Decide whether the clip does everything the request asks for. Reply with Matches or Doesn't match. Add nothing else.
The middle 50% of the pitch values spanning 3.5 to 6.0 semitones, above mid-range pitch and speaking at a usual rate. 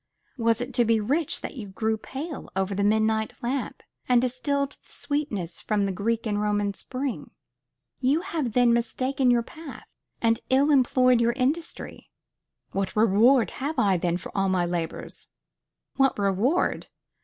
Matches